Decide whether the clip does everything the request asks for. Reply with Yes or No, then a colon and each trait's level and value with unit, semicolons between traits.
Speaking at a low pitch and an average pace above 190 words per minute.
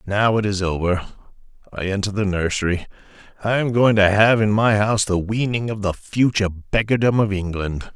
No: low, 100 Hz; average, 180 wpm